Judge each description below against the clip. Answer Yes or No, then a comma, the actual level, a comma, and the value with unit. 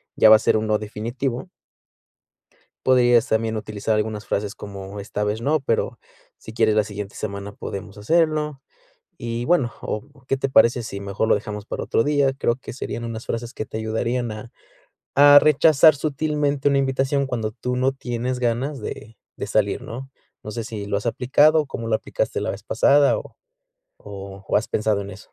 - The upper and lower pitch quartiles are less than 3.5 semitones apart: No, average, 4.0 semitones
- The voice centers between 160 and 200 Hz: No, low, 115 Hz